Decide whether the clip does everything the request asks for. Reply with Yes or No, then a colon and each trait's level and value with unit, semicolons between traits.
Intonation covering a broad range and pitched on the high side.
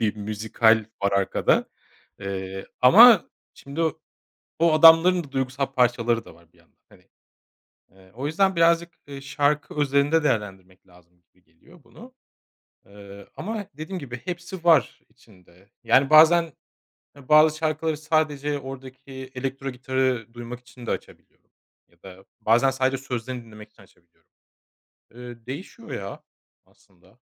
No: wide, 6.1 semitones; low, 130 Hz